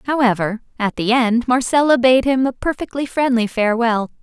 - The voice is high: Yes, high, 245 Hz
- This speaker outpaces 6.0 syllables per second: No, 5.1 syllables/s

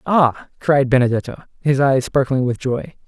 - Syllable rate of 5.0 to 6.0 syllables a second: No, 4.6 syllables/s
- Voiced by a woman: No, male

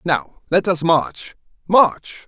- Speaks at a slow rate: Yes, slow, 130 wpm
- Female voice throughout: No, male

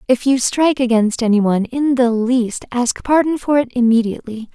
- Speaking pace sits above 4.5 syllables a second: Yes, 5.4 syllables/s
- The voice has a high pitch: Yes, high, 245 Hz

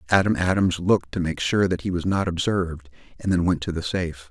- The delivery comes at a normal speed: No, fast, 235 wpm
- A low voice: Yes, very low, 90 Hz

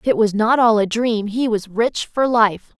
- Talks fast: Yes, fast, 255 wpm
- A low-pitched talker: No, high, 220 Hz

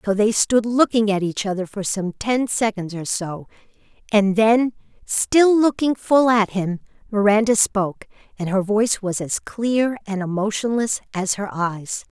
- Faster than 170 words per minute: No, average, 165 wpm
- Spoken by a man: No, female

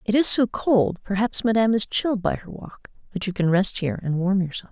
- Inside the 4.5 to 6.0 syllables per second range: Yes, 5.8 syllables/s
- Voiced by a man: No, female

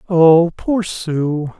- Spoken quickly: No, slow, 115 wpm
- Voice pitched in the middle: Yes, medium, 170 Hz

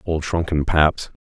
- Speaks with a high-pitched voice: No, very low, 80 Hz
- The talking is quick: No, average, 145 wpm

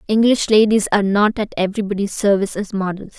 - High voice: Yes, high, 205 Hz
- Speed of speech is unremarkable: Yes, average, 170 wpm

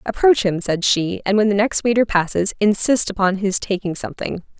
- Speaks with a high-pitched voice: Yes, high, 200 Hz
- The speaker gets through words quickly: No, average, 195 wpm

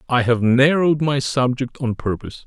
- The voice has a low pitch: Yes, low, 130 Hz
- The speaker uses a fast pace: No, average, 170 wpm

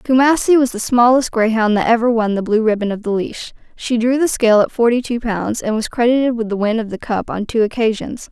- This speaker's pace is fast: Yes, fast, 245 wpm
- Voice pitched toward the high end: Yes, high, 230 Hz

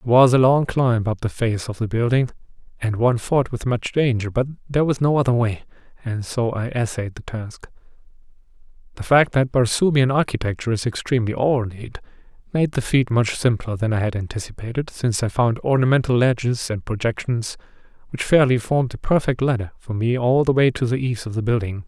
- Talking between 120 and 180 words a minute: No, average, 190 wpm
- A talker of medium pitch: No, low, 120 Hz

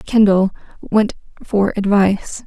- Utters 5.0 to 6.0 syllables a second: No, 4.0 syllables/s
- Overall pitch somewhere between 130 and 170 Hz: No, high, 200 Hz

